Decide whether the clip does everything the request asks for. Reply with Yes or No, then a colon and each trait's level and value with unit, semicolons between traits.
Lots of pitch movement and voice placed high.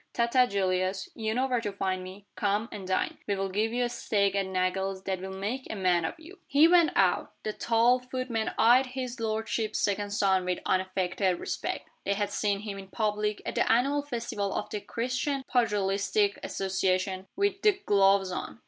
No: average, 3.9 semitones; high, 205 Hz